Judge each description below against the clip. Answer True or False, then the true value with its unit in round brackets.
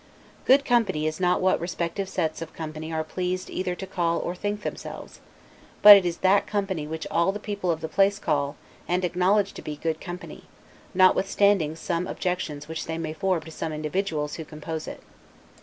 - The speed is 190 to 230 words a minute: True (195 wpm)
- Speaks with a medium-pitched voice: True (175 Hz)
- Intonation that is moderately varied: True (3.3 semitones)